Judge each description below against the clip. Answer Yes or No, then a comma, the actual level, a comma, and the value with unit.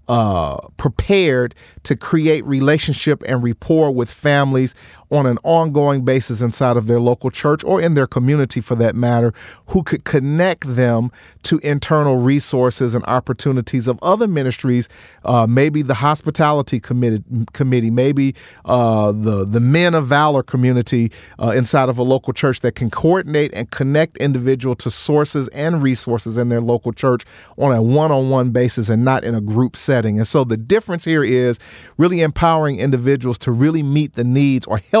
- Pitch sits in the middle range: No, low, 130 Hz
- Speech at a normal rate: Yes, average, 165 wpm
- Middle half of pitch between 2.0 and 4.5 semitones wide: Yes, average, 3.5 semitones